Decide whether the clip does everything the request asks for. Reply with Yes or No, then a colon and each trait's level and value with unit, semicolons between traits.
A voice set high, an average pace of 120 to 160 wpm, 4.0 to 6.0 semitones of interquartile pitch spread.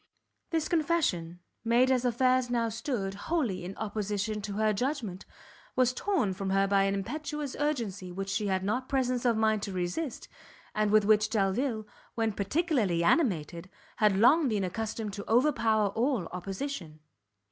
Yes: high, 215 Hz; average, 155 wpm; average, 4.7 semitones